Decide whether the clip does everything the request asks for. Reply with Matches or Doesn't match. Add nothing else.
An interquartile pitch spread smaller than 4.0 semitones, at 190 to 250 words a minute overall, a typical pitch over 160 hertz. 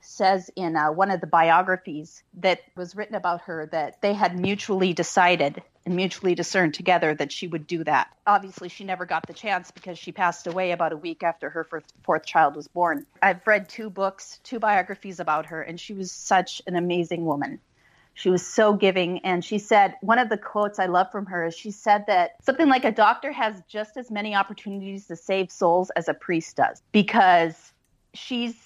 Matches